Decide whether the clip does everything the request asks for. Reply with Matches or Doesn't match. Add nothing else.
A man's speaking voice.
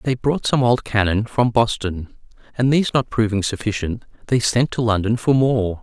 Matches